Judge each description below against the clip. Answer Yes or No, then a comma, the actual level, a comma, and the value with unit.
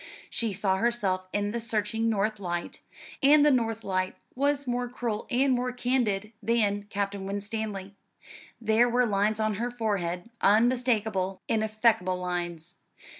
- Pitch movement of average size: Yes, average, 3.4 semitones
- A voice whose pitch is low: No, high, 215 Hz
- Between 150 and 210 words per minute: No, slow, 135 wpm